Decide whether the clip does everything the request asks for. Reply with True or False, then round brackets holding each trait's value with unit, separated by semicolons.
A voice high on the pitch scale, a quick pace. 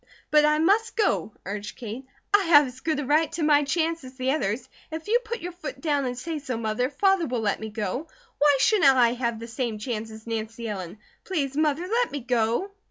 True (275 Hz; 225 wpm)